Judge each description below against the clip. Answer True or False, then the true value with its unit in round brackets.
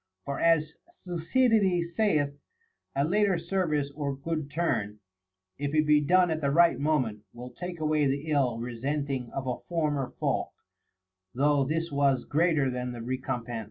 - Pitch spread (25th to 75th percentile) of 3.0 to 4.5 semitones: True (3.8 semitones)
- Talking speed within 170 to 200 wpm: False (155 wpm)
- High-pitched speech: False (150 Hz)